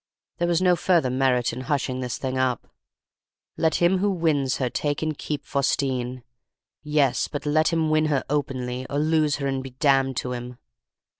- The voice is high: No, medium, 140 Hz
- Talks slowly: No, average, 180 wpm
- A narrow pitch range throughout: No, average, 3.3 semitones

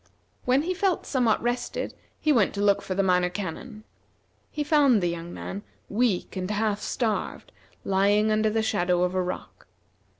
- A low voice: No, high, 210 Hz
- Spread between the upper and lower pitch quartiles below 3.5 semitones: No, average, 4.6 semitones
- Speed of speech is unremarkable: Yes, average, 170 wpm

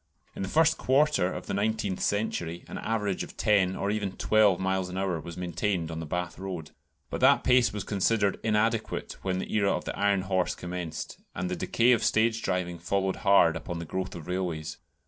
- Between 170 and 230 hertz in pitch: No, very low, 95 Hz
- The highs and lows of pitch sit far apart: No, average, 3.0 semitones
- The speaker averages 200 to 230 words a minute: Yes, fast, 205 wpm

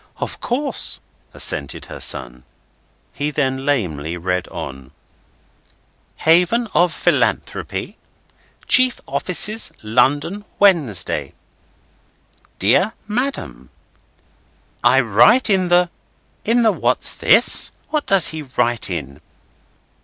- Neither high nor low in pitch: Yes, medium, 150 Hz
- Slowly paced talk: Yes, slow, 95 wpm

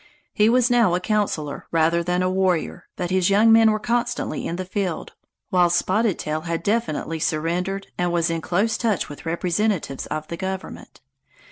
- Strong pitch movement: No, average, 4.1 semitones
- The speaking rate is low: No, average, 175 wpm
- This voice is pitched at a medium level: Yes, medium, 180 Hz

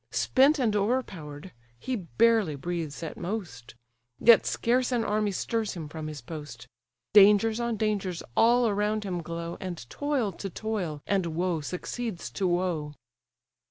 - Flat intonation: No, average, 5.1 semitones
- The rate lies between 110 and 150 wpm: Yes, average, 145 wpm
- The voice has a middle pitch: No, high, 195 Hz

